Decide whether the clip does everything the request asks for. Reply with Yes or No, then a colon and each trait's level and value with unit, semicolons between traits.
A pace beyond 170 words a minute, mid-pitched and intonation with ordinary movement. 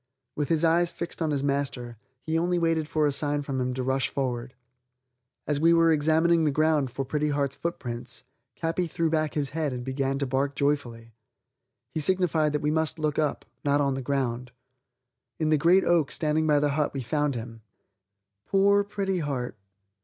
Yes: average, 190 wpm; medium, 150 Hz; average, 3.0 semitones